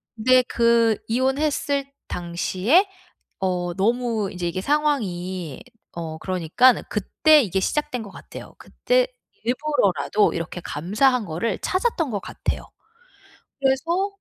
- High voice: Yes, high, 230 Hz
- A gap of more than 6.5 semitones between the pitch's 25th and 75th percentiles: Yes, wide, 7.3 semitones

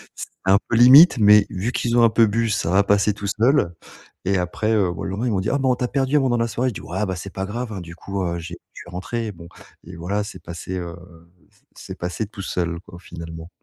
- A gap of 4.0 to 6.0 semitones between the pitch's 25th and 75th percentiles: Yes, average, 4.6 semitones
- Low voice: Yes, low, 100 Hz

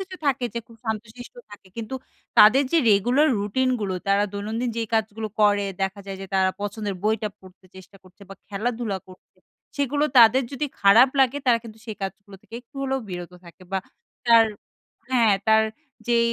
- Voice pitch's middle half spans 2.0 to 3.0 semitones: No, average, 3.5 semitones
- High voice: Yes, high, 220 Hz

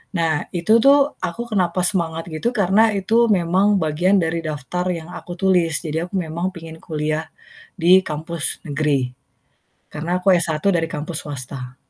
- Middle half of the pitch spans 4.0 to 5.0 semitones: No, average, 3.0 semitones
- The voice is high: No, medium, 170 Hz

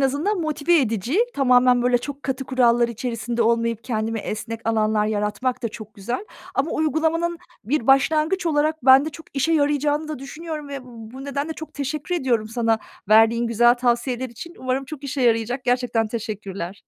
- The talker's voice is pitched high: Yes, very high, 255 Hz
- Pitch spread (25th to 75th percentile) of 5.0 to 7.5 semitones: No, average, 4.3 semitones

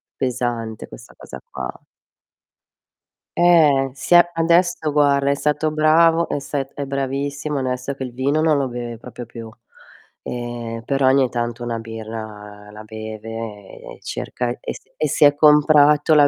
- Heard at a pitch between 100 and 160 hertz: Yes, low, 135 Hz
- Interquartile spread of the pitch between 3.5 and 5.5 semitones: Yes, average, 4.3 semitones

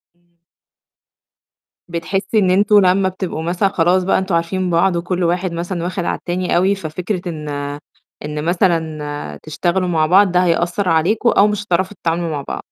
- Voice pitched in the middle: Yes, medium, 175 Hz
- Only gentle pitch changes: Yes, narrow, 2.2 semitones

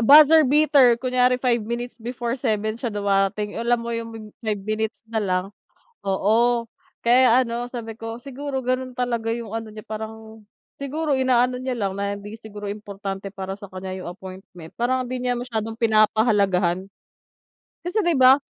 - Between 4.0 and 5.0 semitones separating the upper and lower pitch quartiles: No, average, 3.3 semitones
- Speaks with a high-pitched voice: Yes, high, 225 Hz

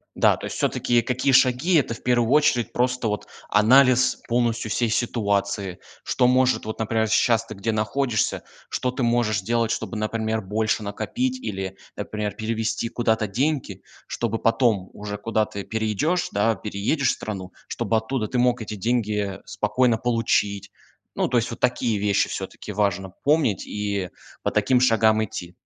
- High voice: No, low, 110 Hz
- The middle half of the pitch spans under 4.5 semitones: Yes, average, 2.9 semitones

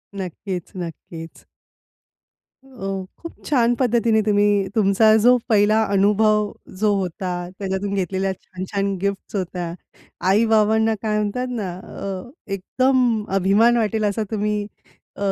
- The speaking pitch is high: Yes, high, 205 Hz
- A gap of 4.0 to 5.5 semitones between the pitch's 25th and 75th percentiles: No, narrow, 2.4 semitones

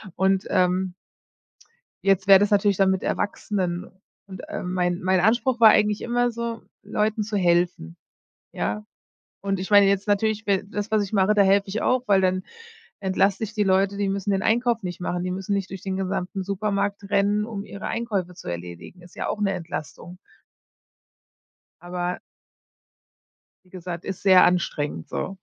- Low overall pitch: No, high, 195 Hz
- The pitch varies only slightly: Yes, narrow, 2.2 semitones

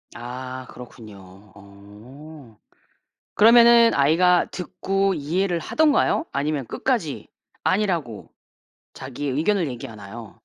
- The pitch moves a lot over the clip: Yes, wide, 7.8 semitones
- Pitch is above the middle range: No, medium, 140 Hz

